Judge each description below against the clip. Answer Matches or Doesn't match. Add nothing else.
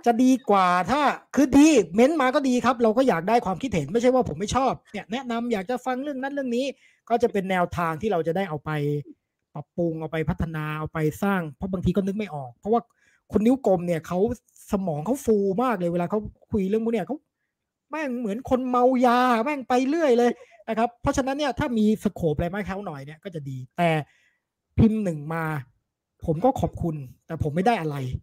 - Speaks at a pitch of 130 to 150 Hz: Doesn't match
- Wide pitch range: Matches